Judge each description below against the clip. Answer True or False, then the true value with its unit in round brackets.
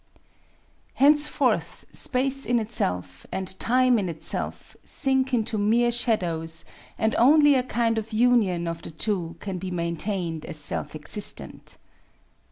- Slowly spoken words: True (130 wpm)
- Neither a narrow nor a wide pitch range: False (6.6 semitones)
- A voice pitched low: False (215 Hz)